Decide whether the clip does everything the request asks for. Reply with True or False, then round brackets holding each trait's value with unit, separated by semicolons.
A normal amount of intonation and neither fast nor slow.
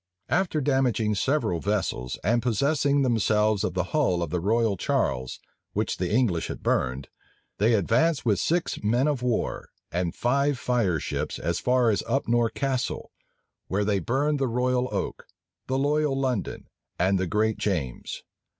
False (5.7 semitones; 150 wpm)